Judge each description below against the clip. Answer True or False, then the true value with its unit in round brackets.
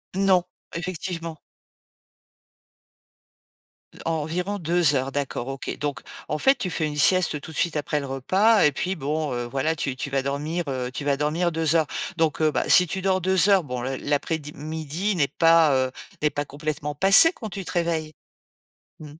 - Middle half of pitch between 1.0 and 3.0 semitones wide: False (3.6 semitones)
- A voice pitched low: False (155 Hz)